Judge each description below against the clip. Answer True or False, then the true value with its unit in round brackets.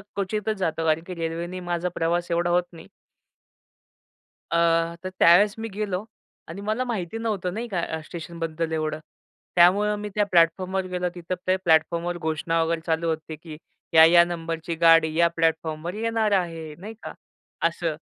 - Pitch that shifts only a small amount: True (2.3 semitones)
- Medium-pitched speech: True (170 Hz)